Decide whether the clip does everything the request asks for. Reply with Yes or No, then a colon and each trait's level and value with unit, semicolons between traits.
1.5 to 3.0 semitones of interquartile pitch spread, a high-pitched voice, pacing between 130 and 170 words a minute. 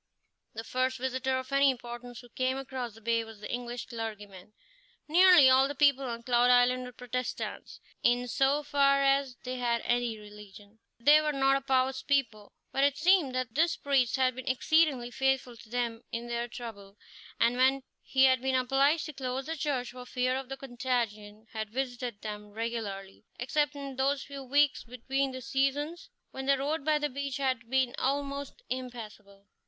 No: narrow, 2.5 semitones; very high, 255 Hz; average, 180 wpm